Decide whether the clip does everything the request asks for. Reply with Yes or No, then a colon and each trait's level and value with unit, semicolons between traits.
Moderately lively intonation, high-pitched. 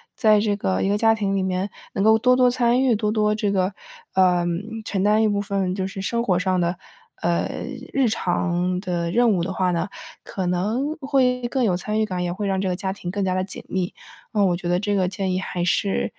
Yes: average, 3.0 semitones; high, 195 Hz